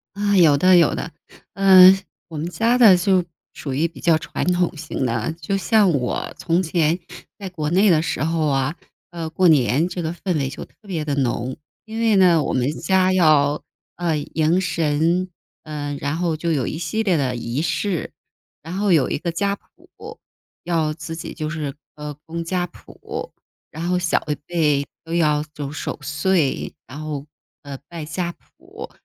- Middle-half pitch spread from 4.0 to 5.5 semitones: No, average, 3.5 semitones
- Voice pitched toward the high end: No, medium, 165 Hz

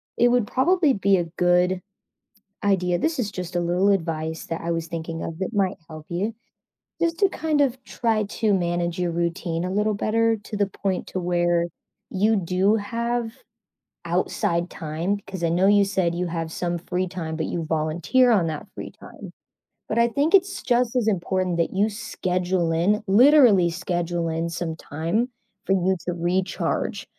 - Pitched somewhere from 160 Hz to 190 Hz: Yes, medium, 185 Hz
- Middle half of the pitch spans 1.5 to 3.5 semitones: No, average, 4.0 semitones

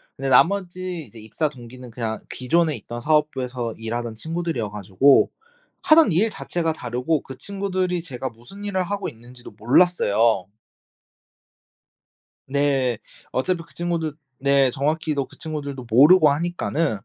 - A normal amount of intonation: No, wide, 5.9 semitones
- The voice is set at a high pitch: No, medium, 140 Hz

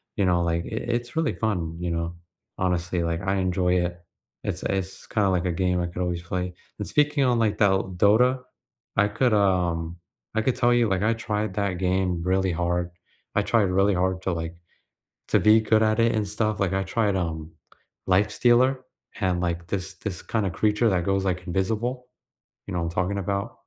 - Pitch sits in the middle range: No, very low, 95 Hz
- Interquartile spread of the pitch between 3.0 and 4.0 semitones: Yes, average, 3.5 semitones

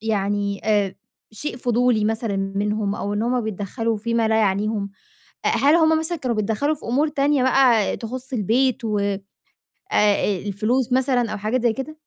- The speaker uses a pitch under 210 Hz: No, high, 225 Hz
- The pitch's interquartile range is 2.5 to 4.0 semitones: Yes, average, 3.7 semitones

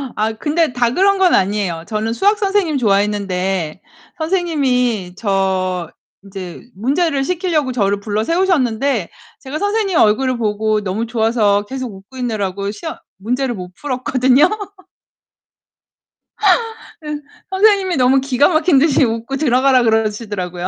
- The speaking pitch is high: Yes, high, 240 Hz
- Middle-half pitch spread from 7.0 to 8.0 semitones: No, wide, 6.4 semitones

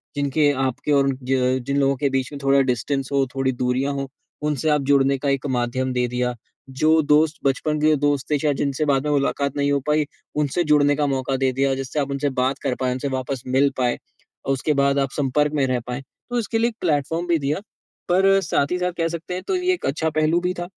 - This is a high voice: No, medium, 140 Hz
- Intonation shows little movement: Yes, narrow, 2.3 semitones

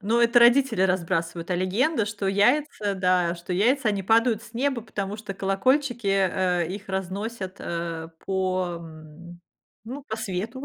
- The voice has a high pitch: Yes, high, 195 Hz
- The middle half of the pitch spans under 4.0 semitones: No, average, 4.3 semitones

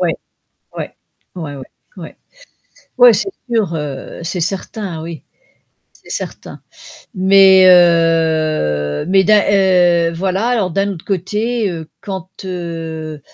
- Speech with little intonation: No, average, 3.2 semitones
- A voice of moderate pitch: Yes, medium, 180 Hz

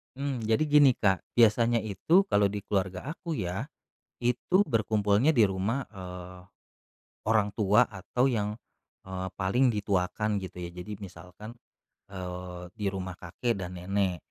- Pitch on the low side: Yes, low, 100 Hz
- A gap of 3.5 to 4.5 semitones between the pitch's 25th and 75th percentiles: Yes, average, 4.0 semitones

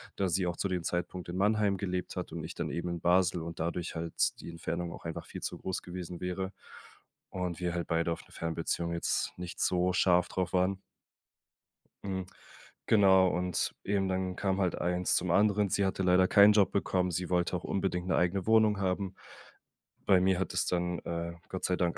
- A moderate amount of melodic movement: No, narrow, 1.5 semitones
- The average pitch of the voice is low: Yes, very low, 90 Hz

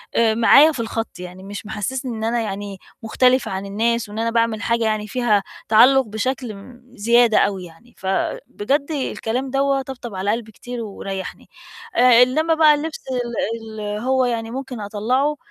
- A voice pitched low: No, high, 230 Hz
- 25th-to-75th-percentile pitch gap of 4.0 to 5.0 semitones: No, average, 3.5 semitones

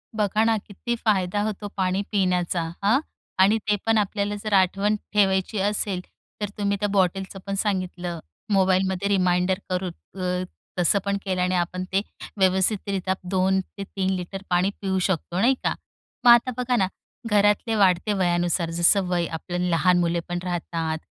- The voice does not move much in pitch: Yes, narrow, 2.1 semitones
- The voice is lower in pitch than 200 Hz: Yes, high, 190 Hz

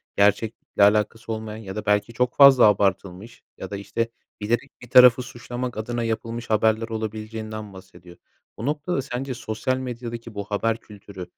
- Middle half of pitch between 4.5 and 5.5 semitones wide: No, average, 2.7 semitones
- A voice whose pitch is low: Yes, low, 110 Hz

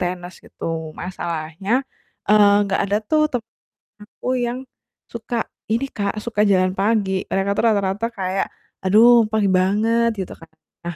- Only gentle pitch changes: No, average, 3.1 semitones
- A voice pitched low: No, high, 200 Hz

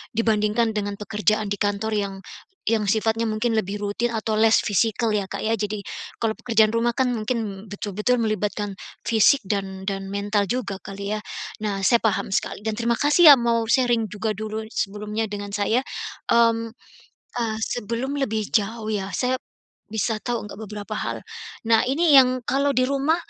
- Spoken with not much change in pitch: Yes, narrow, 2.2 semitones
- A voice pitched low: No, high, 220 Hz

